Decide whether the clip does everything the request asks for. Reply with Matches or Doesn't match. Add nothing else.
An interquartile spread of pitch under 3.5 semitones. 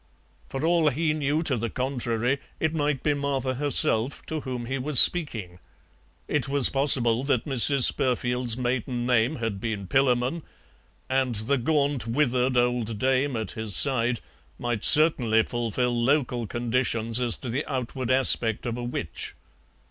Matches